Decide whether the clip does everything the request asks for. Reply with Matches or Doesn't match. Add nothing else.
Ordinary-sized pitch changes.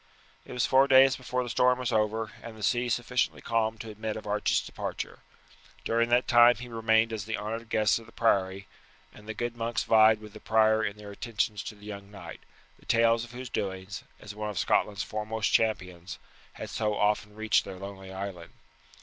Doesn't match